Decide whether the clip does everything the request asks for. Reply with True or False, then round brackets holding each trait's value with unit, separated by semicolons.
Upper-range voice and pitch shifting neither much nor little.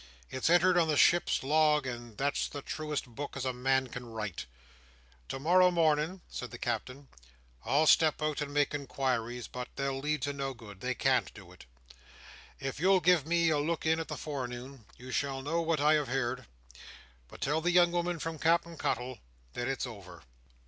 False (140 Hz; 4.0 semitones)